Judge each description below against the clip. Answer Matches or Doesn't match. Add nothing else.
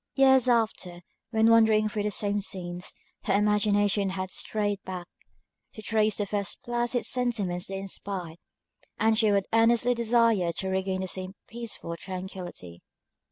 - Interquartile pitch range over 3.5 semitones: Doesn't match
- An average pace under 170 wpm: Matches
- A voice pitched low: Doesn't match